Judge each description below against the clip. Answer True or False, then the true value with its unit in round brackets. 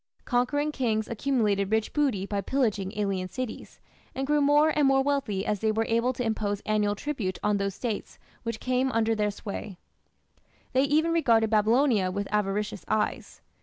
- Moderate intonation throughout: True (4.5 semitones)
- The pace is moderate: True (165 wpm)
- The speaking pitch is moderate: False (220 Hz)